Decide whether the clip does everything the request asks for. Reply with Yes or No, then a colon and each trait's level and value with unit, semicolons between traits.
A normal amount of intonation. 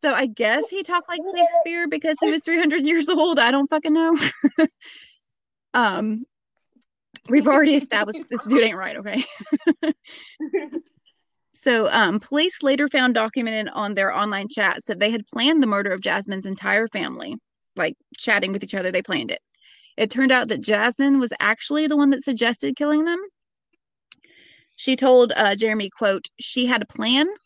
No: wide, 6.2 semitones